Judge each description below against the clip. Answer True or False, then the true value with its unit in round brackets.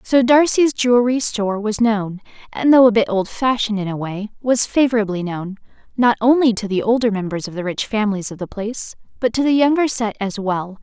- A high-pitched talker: True (220 Hz)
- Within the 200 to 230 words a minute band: True (205 wpm)